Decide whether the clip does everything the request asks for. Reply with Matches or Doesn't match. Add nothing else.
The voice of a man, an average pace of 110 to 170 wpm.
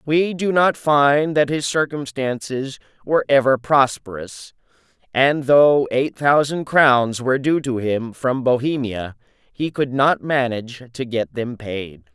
Matches